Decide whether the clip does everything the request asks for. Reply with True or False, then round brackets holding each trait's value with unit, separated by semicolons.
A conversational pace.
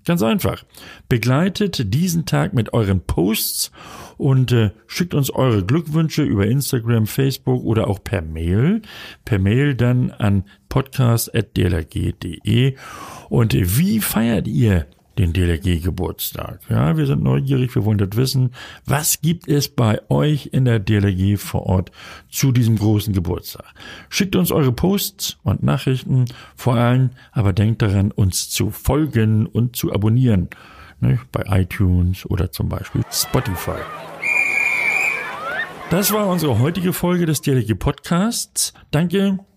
True (135 wpm)